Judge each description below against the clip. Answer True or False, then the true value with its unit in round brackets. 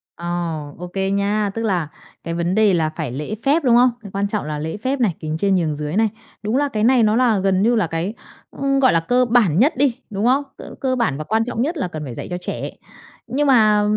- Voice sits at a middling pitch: False (210 Hz)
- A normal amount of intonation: False (6.2 semitones)